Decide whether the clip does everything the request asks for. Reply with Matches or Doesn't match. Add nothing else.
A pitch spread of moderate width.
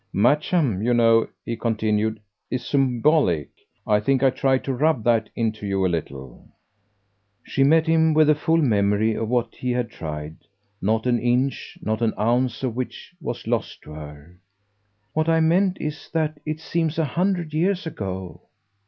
Doesn't match